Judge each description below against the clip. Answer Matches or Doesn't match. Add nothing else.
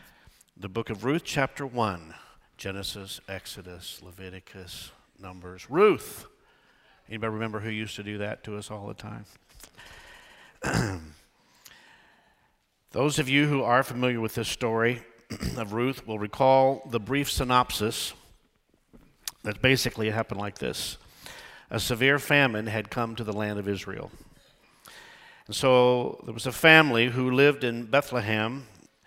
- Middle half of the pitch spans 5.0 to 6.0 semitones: Doesn't match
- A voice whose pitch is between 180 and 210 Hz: Doesn't match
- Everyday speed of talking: Doesn't match